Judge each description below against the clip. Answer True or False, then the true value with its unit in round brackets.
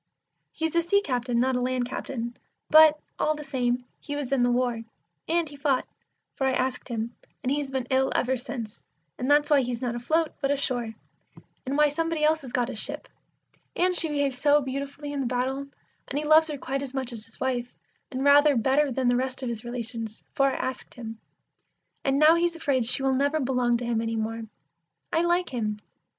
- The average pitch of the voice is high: True (265 Hz)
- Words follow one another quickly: True (210 wpm)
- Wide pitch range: False (3.1 semitones)